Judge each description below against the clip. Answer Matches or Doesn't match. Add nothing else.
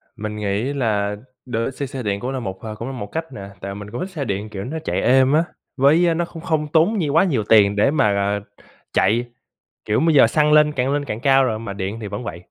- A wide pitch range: Matches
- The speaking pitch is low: Matches